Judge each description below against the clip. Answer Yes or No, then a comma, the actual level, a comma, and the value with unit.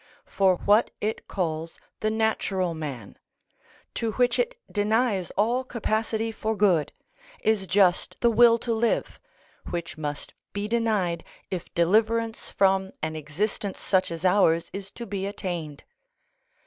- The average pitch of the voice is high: Yes, high, 200 Hz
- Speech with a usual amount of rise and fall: Yes, average, 4.2 semitones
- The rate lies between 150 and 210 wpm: No, slow, 135 wpm